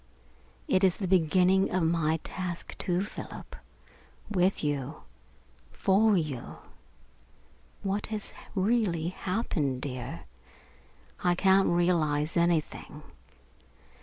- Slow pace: Yes, slow, 95 wpm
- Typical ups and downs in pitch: Yes, average, 3.7 semitones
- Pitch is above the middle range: No, medium, 175 Hz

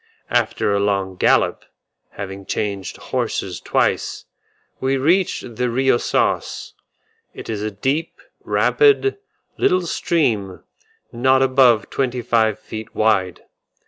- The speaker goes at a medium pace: No, slow, 110 wpm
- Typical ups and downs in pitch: Yes, average, 4.7 semitones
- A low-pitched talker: Yes, low, 115 Hz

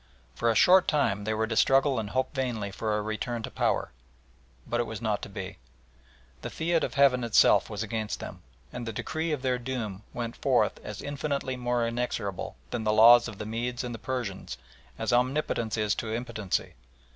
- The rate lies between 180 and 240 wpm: Yes, average, 195 wpm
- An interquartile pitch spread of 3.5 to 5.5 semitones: No, average, 3.1 semitones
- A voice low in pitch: Yes, low, 120 Hz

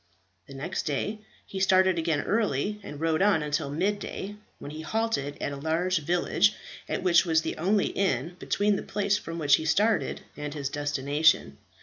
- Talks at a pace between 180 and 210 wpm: Yes, average, 185 wpm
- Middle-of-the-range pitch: Yes, medium, 165 Hz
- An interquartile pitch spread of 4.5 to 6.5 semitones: Yes, average, 5.2 semitones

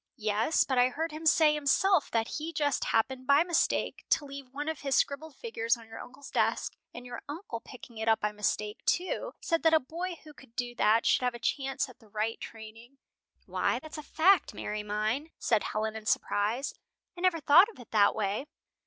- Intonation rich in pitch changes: Yes, wide, 5.8 semitones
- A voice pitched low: No, very high, 260 Hz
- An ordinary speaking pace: No, fast, 215 wpm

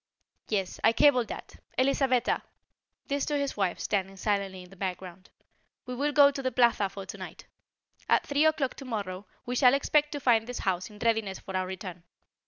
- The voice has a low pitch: No, high, 225 Hz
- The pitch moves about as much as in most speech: No, wide, 6.1 semitones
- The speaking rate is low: No, average, 185 wpm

